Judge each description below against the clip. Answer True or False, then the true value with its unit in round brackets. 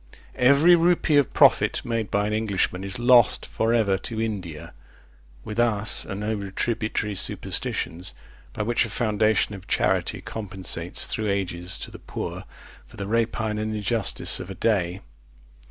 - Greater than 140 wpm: True (155 wpm)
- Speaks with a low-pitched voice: True (105 Hz)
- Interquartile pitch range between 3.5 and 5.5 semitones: False (3.0 semitones)